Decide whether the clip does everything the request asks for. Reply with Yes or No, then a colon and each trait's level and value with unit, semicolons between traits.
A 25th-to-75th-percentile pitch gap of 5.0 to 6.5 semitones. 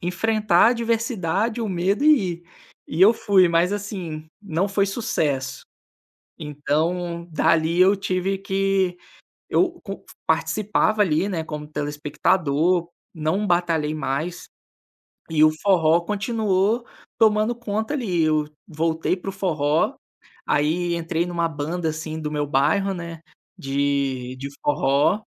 No: average, 4.2 semitones